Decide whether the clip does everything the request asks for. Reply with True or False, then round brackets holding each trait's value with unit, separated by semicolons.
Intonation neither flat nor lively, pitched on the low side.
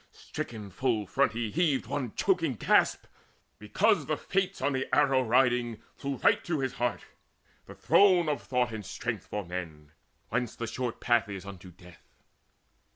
True (4.9 semitones; 120 Hz)